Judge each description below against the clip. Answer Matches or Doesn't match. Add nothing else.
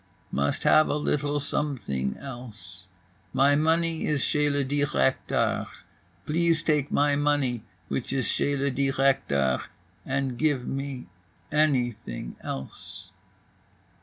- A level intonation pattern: Doesn't match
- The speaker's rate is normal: Doesn't match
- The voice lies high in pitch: Doesn't match